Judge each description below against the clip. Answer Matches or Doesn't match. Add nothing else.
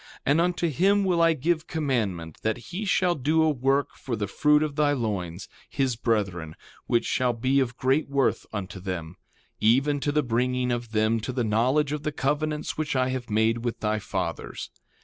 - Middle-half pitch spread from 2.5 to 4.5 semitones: Doesn't match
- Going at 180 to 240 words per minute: Matches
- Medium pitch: Doesn't match